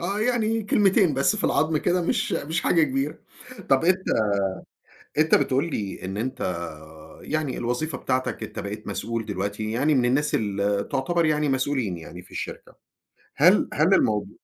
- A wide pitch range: Yes, wide, 7.2 semitones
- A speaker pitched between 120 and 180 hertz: Yes, low, 135 Hz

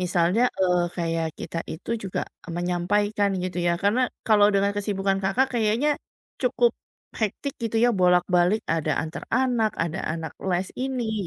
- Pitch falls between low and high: No, high, 195 Hz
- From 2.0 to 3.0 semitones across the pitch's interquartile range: No, average, 3.8 semitones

